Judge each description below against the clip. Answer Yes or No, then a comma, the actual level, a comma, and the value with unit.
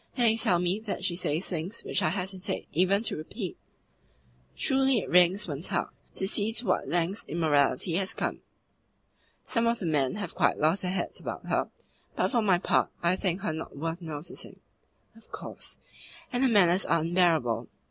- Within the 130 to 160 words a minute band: No, average, 185 wpm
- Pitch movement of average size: Yes, average, 3.7 semitones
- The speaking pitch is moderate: Yes, medium, 180 Hz